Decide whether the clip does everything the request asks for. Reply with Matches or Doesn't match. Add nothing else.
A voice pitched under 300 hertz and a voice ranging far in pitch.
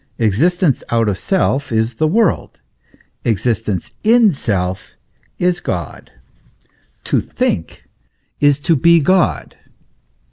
Matches